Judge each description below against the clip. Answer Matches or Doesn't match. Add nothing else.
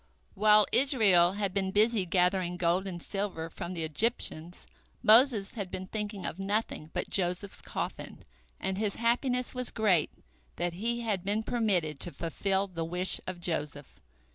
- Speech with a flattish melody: Doesn't match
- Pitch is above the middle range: Matches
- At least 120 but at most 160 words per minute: Matches